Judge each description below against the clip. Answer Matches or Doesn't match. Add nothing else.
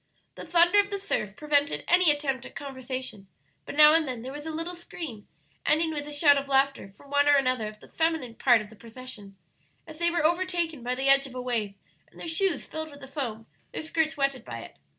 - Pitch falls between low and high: Doesn't match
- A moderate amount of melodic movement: Matches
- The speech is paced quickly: Matches